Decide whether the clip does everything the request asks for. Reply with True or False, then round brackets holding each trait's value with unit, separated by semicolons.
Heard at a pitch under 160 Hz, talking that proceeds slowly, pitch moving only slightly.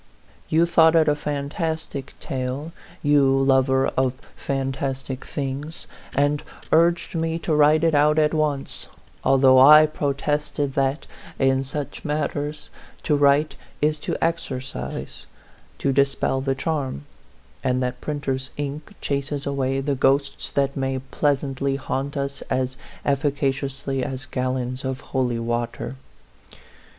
True (140 Hz; 125 wpm; 1.9 semitones)